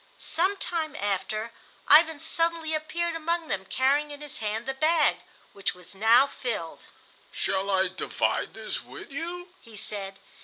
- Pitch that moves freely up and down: Yes, wide, 7.8 semitones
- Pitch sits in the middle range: No, very high, 280 Hz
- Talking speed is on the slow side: No, average, 150 wpm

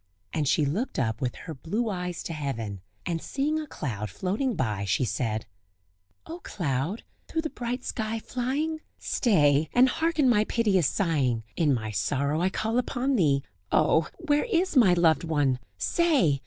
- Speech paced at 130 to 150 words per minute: No, average, 165 wpm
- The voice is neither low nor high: Yes, medium, 175 Hz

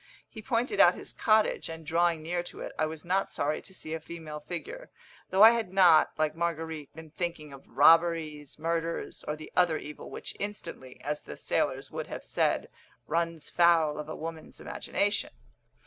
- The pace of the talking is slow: No, average, 180 wpm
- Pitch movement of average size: No, narrow, 2.1 semitones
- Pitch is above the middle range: No, medium, 165 Hz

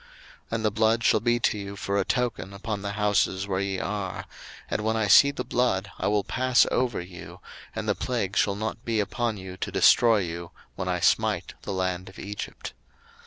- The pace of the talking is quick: Yes, fast, 210 wpm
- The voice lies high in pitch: No, low, 100 Hz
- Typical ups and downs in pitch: Yes, average, 3.0 semitones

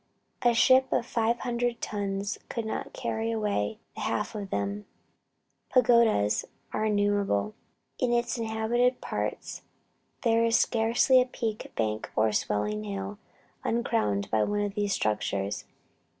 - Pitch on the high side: Yes, high, 210 Hz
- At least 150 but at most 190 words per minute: No, slow, 135 wpm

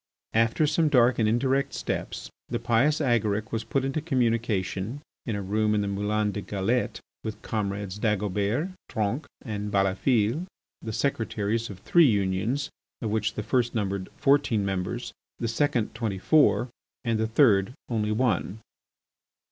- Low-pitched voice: Yes, low, 110 Hz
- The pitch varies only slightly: No, average, 3.4 semitones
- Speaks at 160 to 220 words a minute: No, average, 150 wpm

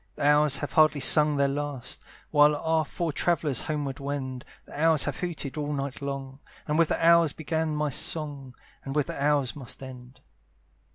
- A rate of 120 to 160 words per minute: No, average, 180 wpm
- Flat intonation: Yes, narrow, 2.0 semitones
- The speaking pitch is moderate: Yes, medium, 145 Hz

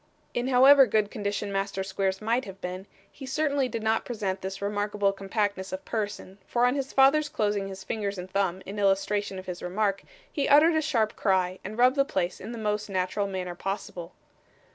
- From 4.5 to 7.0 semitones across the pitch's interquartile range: No, average, 3.8 semitones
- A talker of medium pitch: No, high, 205 Hz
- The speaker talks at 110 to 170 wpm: No, average, 195 wpm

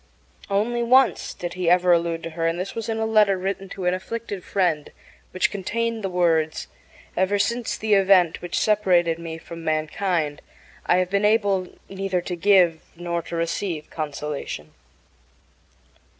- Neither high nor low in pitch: Yes, medium, 180 Hz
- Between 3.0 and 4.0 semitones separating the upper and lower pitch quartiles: Yes, average, 3.3 semitones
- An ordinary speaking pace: Yes, average, 160 wpm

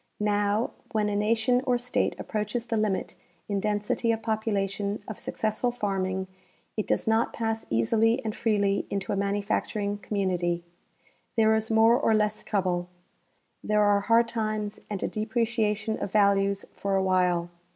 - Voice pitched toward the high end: Yes, high, 210 Hz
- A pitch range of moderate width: No, narrow, 1.9 semitones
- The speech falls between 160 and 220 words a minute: No, average, 150 wpm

